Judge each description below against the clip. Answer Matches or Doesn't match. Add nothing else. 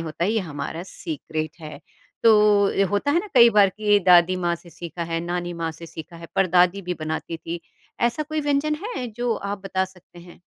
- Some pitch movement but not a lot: Matches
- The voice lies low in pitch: Doesn't match